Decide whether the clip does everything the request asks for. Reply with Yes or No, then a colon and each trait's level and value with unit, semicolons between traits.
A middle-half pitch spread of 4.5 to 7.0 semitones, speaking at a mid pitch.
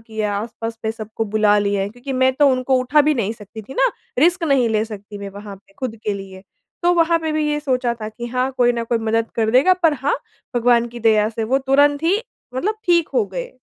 No: average, 4.8 semitones; high, 240 Hz